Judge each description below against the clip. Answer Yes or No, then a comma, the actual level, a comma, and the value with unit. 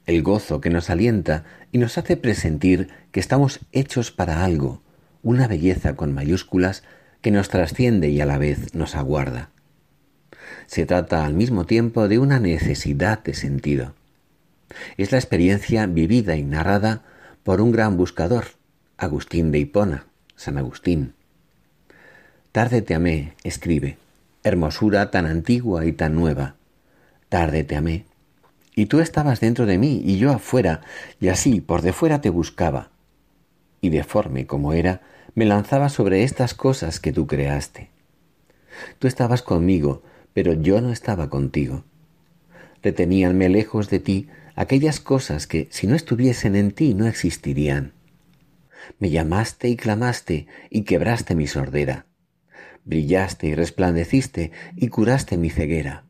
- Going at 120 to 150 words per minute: Yes, average, 140 wpm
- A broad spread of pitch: Yes, wide, 6.6 semitones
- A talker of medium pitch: No, very low, 95 Hz